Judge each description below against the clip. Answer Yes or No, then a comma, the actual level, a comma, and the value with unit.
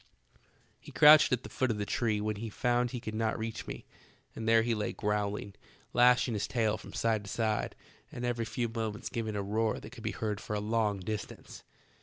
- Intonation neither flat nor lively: No, narrow, 1.8 semitones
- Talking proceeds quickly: Yes, fast, 215 wpm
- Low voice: Yes, low, 110 Hz